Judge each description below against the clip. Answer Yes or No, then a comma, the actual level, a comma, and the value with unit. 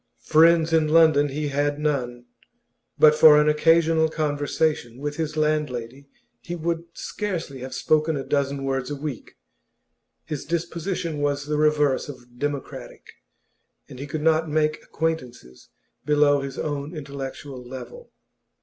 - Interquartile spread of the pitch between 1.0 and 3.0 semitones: Yes, narrow, 2.4 semitones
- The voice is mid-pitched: Yes, medium, 150 Hz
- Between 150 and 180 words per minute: No, average, 140 wpm